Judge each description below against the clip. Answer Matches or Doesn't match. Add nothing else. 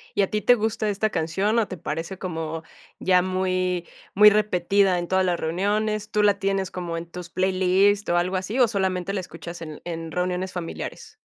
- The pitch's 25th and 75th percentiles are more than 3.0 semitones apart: Doesn't match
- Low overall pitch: Doesn't match